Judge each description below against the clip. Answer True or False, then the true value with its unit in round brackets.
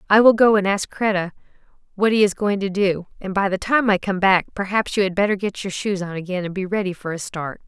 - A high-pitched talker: True (195 Hz)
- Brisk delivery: True (265 wpm)